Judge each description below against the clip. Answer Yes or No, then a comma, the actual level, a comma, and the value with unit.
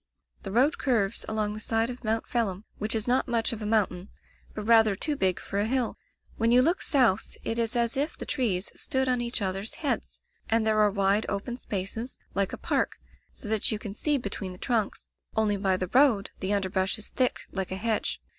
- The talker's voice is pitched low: No, high, 220 Hz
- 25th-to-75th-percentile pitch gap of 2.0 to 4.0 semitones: Yes, average, 3.2 semitones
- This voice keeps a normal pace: No, fast, 215 wpm